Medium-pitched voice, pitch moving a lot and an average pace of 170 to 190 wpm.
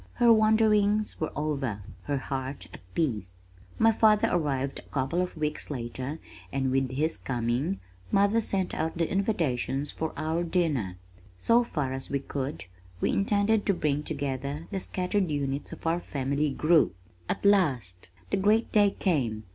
No: medium, 150 Hz; wide, 6.5 semitones; average, 155 wpm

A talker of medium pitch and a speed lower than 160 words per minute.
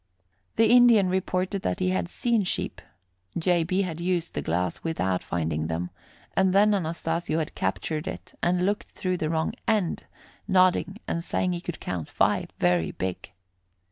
No: medium, 170 Hz; average, 165 wpm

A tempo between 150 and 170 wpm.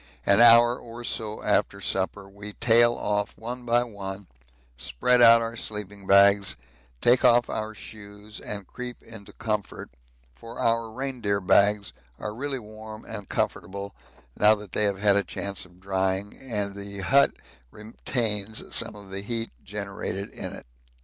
Yes: average, 155 wpm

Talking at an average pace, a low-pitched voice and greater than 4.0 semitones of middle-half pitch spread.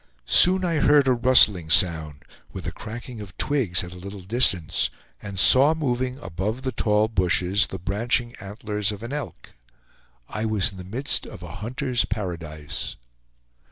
Yes: average, 160 wpm; low, 105 Hz; average, 5.3 semitones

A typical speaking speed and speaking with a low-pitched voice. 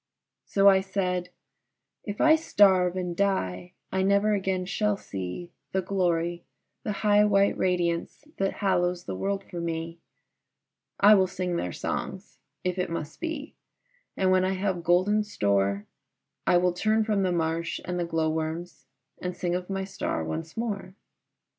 No: average, 160 wpm; medium, 180 Hz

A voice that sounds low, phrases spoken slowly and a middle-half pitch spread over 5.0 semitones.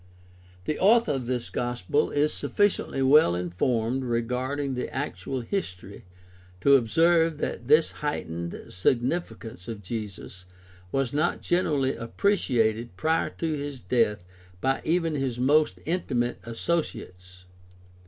Yes: low, 125 Hz; slow, 120 wpm; wide, 5.5 semitones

